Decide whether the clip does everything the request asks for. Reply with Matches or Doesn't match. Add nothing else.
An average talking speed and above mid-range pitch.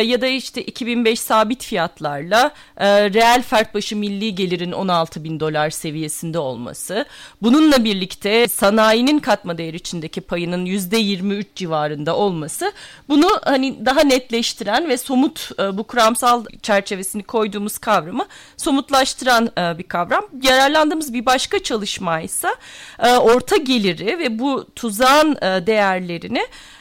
Matches